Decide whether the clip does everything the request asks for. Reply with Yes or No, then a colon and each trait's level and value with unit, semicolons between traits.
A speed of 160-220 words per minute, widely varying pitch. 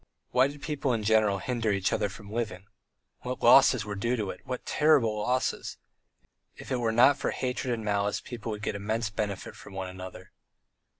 No: average, 190 wpm; average, 3.6 semitones